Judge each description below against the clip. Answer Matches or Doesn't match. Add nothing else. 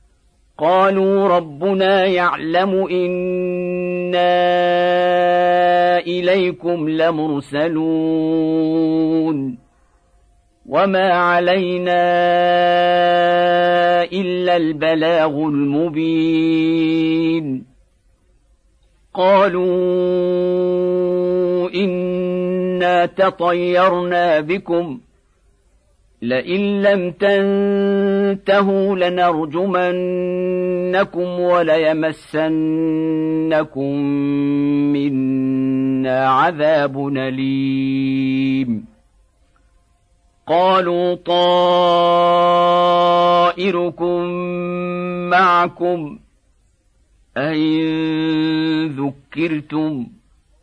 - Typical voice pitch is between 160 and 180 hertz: Matches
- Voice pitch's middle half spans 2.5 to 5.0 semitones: Matches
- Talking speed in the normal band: Doesn't match